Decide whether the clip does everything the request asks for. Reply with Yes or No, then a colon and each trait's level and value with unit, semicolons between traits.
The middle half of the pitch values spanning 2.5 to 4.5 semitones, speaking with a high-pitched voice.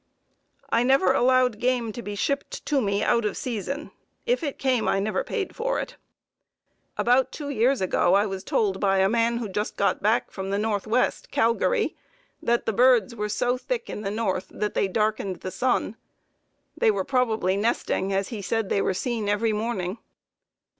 Yes: average, 4.0 semitones; high, 225 Hz